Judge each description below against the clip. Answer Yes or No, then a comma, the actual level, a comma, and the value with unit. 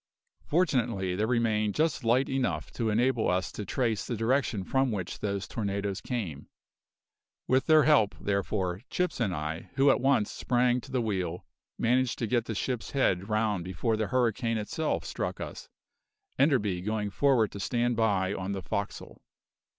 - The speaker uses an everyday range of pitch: Yes, average, 4.2 semitones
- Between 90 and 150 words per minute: No, average, 165 wpm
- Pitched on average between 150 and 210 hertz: No, low, 110 Hz